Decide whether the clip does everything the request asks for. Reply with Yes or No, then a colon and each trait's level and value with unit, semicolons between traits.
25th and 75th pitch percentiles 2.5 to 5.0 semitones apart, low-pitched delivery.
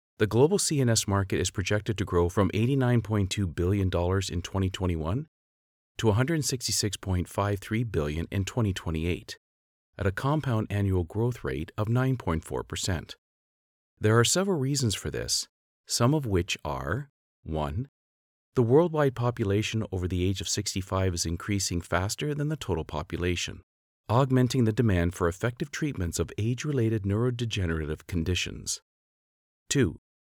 No: wide, 5.6 semitones; low, 100 Hz